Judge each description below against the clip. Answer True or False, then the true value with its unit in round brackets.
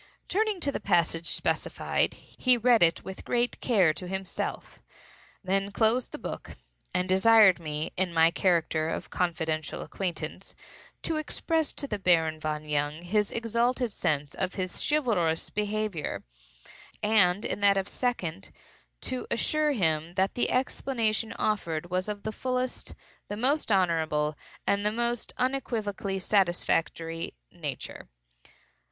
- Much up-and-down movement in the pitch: True (5.7 semitones)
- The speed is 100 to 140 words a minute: True (135 wpm)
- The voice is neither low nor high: False (195 Hz)